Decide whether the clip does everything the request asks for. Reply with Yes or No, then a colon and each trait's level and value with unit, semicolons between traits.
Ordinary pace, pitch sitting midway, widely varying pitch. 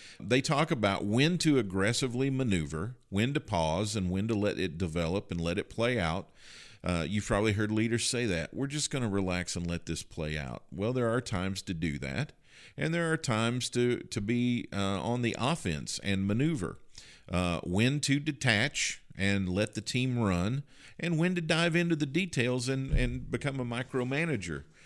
No: average, 190 wpm; low, 115 Hz; wide, 5.7 semitones